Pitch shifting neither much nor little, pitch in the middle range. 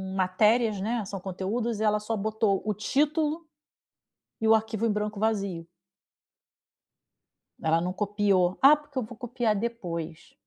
No: average, 3.2 semitones; high, 215 Hz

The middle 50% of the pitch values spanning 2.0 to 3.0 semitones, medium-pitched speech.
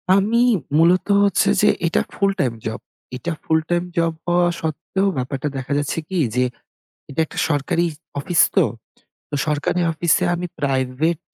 No: average, 3.8 semitones; medium, 165 Hz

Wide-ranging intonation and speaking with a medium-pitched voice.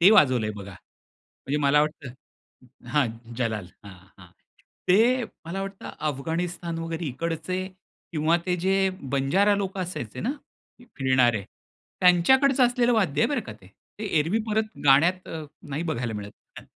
Yes: wide, 6.6 semitones; medium, 165 Hz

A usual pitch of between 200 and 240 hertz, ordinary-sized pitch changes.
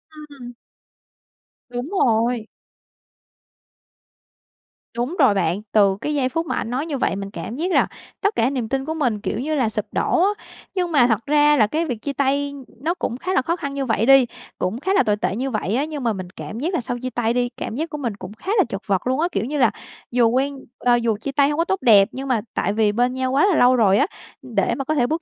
No: very high, 255 Hz; average, 4.8 semitones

